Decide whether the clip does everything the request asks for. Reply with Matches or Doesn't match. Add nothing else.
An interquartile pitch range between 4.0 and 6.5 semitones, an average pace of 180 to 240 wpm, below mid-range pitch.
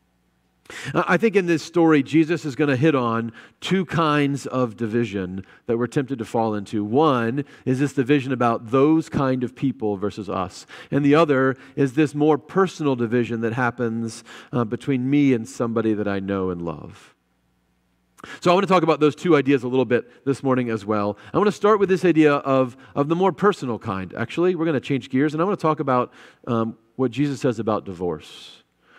Matches